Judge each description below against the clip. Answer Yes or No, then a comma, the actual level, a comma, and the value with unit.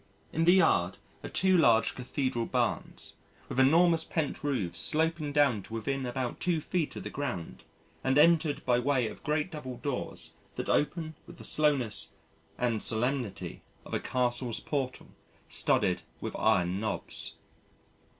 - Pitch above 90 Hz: Yes, low, 135 Hz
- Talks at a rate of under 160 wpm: Yes, average, 150 wpm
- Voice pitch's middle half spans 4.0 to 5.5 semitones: Yes, average, 4.6 semitones